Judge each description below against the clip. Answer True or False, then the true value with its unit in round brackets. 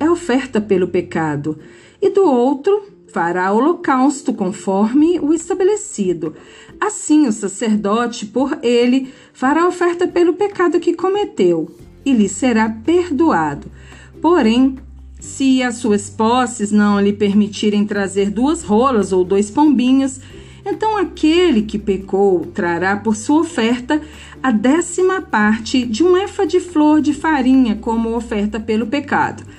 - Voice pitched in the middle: False (250 Hz)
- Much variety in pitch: True (7.7 semitones)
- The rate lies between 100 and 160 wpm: True (130 wpm)